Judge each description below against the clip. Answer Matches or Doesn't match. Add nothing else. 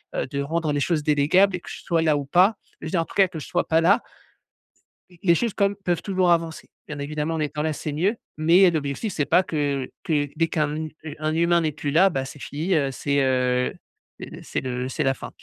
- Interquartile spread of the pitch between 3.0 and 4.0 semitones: Matches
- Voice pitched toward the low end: Doesn't match